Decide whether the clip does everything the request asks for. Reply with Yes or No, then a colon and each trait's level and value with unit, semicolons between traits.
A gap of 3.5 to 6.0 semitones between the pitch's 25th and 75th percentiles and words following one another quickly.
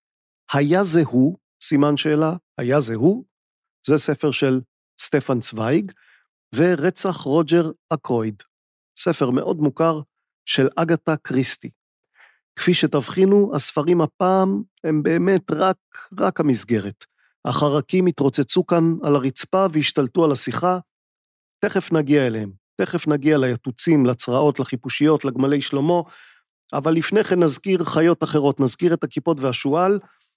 No: average, 4.0 semitones; average, 115 wpm